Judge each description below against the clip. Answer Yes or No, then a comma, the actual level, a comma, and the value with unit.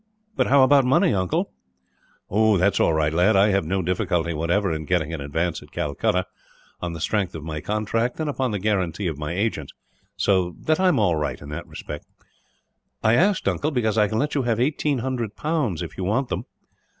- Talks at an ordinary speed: No, fast, 210 wpm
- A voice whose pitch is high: No, low, 100 Hz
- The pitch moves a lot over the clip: Yes, wide, 6.2 semitones